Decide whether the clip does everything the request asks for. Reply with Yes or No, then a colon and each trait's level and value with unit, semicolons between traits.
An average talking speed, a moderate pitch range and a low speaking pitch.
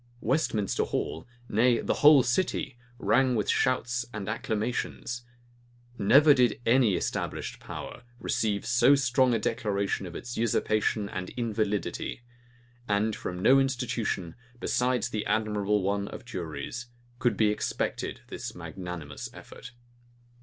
No: slow, 125 wpm; average, 3.4 semitones; low, 115 Hz